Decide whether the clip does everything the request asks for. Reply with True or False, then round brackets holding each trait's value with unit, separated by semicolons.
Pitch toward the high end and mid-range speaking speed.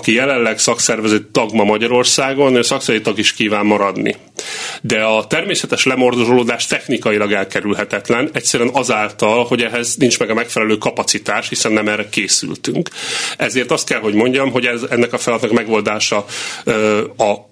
False (115 Hz; 145 wpm)